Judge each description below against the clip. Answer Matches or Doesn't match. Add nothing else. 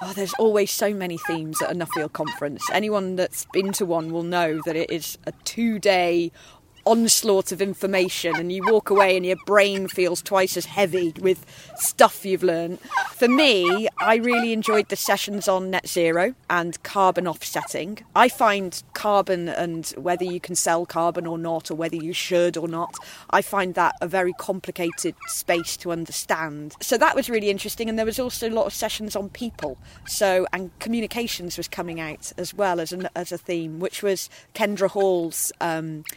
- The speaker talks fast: Doesn't match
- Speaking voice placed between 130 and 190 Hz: Matches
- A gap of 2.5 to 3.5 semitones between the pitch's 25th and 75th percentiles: Matches